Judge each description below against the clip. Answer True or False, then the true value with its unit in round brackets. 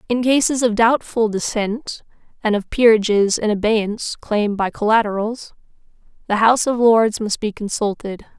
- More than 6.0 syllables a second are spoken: False (4.9 syllables/s)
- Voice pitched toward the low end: False (220 Hz)